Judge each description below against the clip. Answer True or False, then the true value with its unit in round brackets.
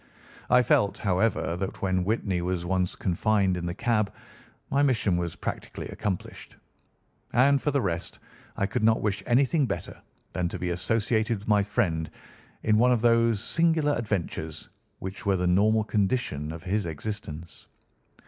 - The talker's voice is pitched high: False (100 Hz)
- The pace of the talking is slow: False (160 wpm)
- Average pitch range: True (4.3 semitones)